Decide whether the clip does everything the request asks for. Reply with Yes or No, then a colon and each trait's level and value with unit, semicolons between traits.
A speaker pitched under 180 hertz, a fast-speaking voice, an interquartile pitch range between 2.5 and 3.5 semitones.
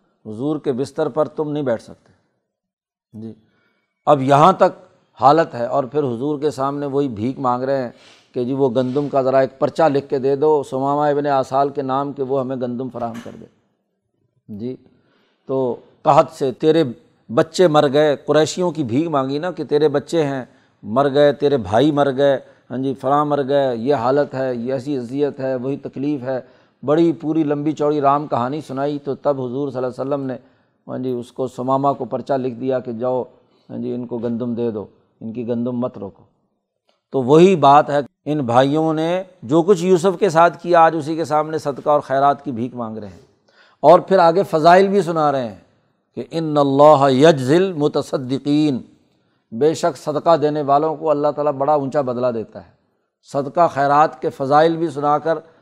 Yes: medium, 140 Hz; fast, 195 wpm; average, 2.8 semitones